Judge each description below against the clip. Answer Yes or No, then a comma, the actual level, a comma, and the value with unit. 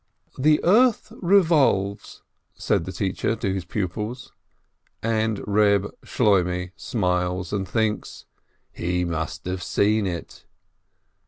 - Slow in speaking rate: Yes, slow, 105 wpm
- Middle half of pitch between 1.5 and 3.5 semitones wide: No, average, 3.9 semitones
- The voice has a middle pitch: No, low, 100 Hz